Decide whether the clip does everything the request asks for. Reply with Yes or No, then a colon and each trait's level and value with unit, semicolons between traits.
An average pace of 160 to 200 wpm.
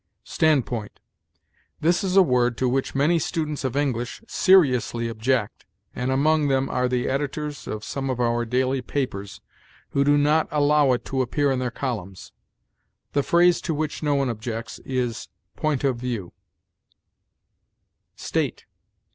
No: average, 145 wpm